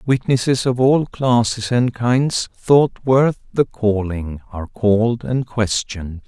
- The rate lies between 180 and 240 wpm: No, slow, 135 wpm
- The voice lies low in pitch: Yes, low, 120 Hz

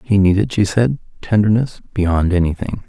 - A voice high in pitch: No, low, 100 Hz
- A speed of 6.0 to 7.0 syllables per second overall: No, 4.9 syllables/s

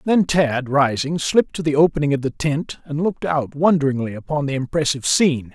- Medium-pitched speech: Yes, medium, 145 Hz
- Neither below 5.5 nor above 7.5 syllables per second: Yes, 5.8 syllables/s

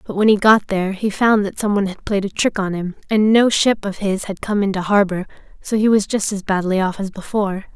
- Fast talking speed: Yes, fast, 265 wpm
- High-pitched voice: Yes, high, 200 Hz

